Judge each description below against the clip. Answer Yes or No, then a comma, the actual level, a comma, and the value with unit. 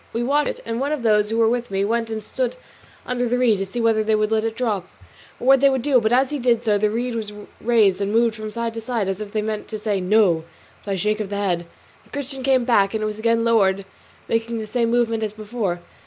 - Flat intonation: Yes, narrow, 2.3 semitones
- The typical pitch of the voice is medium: No, high, 225 Hz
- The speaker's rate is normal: No, fast, 275 wpm